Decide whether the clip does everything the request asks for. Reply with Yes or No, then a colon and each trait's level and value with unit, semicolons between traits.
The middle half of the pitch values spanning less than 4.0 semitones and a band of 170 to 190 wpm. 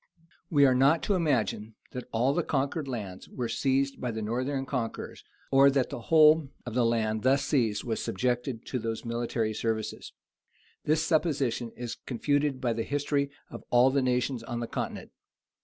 Yes: average, 3.3 semitones; average, 175 wpm